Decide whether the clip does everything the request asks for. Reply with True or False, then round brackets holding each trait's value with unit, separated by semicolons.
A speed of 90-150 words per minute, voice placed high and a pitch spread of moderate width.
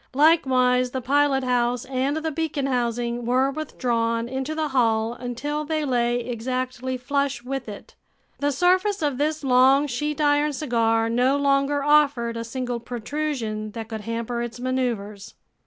True (145 wpm; 255 Hz; 3.3 semitones)